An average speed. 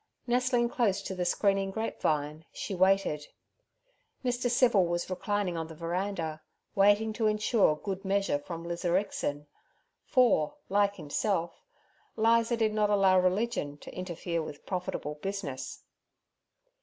No: slow, 130 wpm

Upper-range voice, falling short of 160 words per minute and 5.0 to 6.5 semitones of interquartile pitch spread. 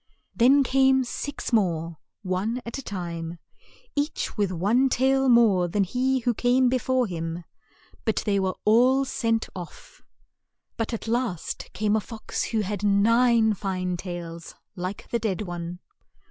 Yes: high, 215 Hz; average, 150 wpm; average, 5.3 semitones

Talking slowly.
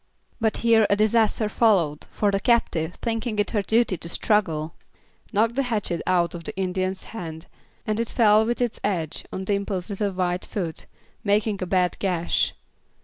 No: average, 170 wpm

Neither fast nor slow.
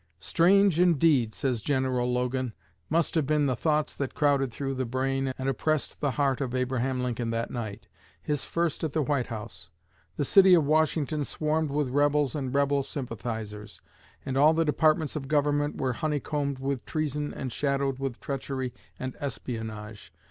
Yes: average, 165 wpm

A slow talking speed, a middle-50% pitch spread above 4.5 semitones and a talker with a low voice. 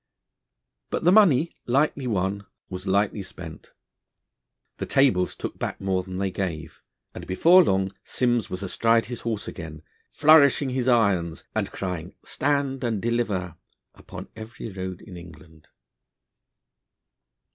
Yes: slow, 130 wpm; average, 5.3 semitones; low, 100 Hz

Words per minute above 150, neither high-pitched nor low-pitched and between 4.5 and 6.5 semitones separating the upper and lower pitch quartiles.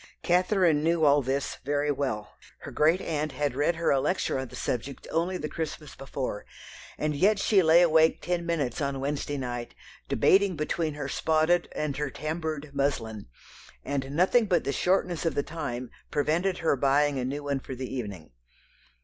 No: average, 175 wpm; medium, 150 Hz; average, 3.5 semitones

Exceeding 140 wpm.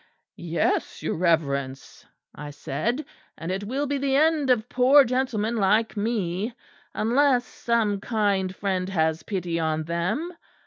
No: slow, 135 wpm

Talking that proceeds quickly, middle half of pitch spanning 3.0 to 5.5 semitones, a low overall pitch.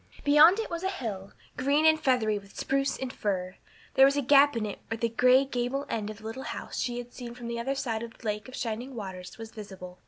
No: fast, 250 wpm; average, 4.1 semitones; high, 240 Hz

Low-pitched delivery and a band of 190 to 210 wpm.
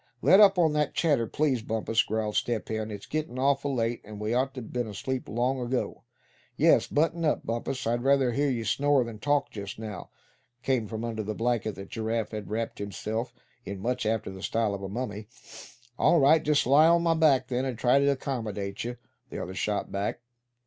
Yes: low, 120 Hz; fast, 205 wpm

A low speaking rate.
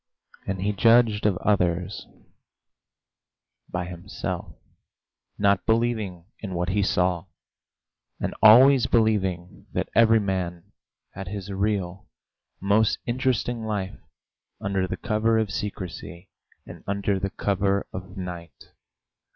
Yes: slow, 110 wpm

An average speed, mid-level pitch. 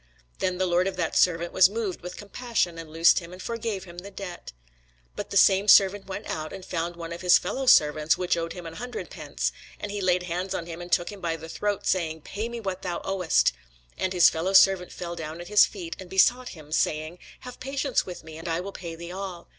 No: fast, 235 wpm; medium, 180 Hz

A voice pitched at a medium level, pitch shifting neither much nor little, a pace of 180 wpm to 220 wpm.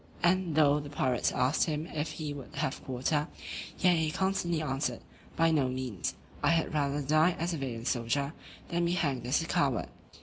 Yes: medium, 150 Hz; average, 3.7 semitones; average, 190 wpm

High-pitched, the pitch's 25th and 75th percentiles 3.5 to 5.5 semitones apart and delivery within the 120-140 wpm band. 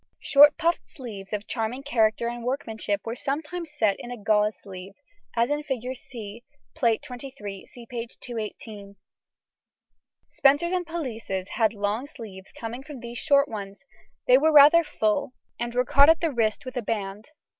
No: high, 240 Hz; average, 4.6 semitones; average, 165 wpm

